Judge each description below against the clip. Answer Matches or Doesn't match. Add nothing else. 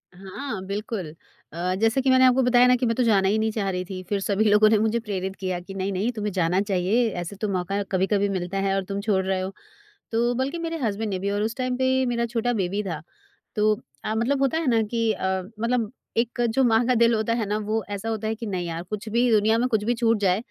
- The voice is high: Matches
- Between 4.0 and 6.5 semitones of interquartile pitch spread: Doesn't match